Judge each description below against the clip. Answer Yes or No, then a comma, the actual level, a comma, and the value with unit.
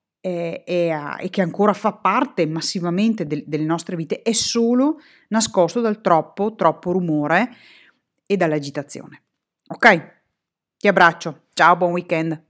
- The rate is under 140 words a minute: Yes, average, 130 wpm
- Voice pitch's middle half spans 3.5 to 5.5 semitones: Yes, average, 4.6 semitones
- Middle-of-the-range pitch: Yes, medium, 180 Hz